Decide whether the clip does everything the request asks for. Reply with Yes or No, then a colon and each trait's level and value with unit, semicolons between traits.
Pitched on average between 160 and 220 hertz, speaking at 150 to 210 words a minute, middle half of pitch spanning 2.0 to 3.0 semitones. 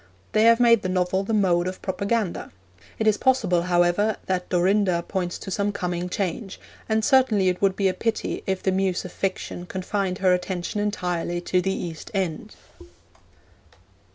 Yes: high, 190 Hz; average, 170 wpm; narrow, 2.4 semitones